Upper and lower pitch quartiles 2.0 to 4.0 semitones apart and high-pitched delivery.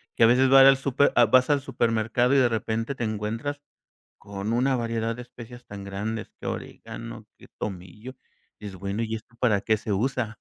No: average, 3.0 semitones; low, 115 Hz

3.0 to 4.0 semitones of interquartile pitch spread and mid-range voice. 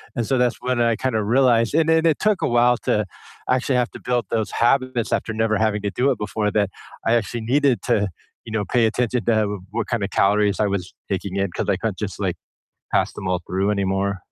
No: average, 3.3 semitones; low, 110 Hz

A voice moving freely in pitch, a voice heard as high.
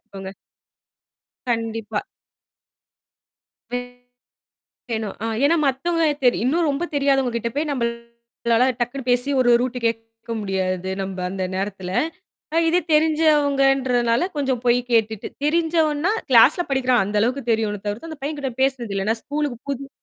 No: average, 4.1 semitones; high, 245 Hz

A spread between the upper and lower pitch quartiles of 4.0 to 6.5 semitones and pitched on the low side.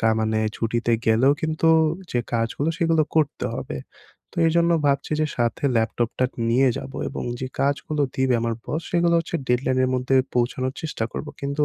Yes: average, 4.6 semitones; low, 130 Hz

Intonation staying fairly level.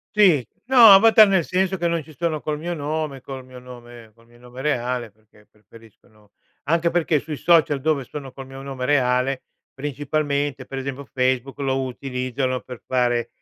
No: average, 3.5 semitones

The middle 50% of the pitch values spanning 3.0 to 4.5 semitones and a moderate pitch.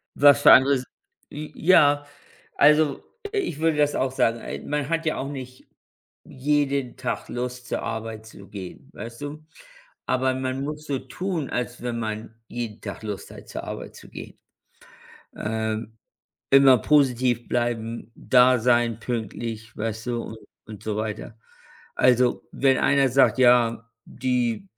No: average, 3.6 semitones; low, 125 Hz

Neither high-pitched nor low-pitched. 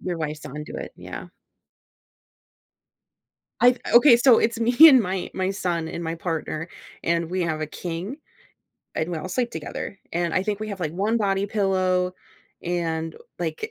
Yes: medium, 180 Hz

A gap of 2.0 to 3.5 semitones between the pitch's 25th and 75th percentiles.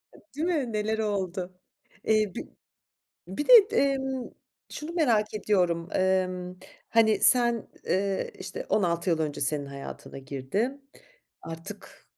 No: wide, 5.5 semitones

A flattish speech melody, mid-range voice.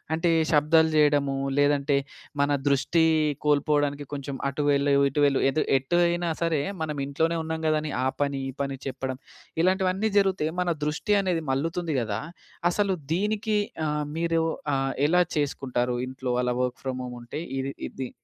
No: average, 3.4 semitones; medium, 150 Hz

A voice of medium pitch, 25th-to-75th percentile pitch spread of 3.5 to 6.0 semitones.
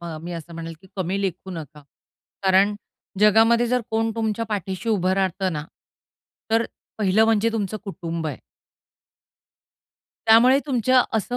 No: high, 200 Hz; average, 4.2 semitones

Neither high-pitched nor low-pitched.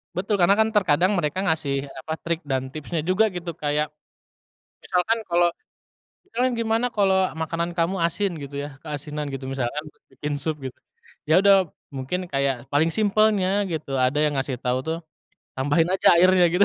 Yes: medium, 165 Hz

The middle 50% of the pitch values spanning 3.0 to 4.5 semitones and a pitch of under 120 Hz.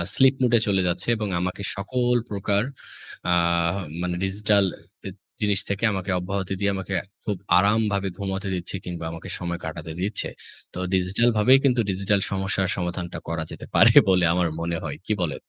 No: narrow, 2.4 semitones; very low, 95 Hz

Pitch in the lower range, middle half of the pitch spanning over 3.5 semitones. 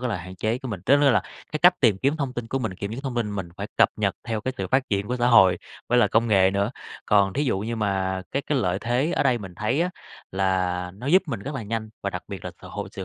Yes: low, 115 Hz; average, 5.1 semitones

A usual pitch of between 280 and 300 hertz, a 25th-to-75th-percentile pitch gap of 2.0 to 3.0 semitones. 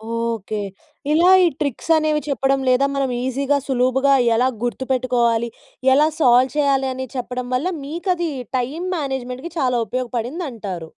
No: very high, 260 Hz; average, 2.7 semitones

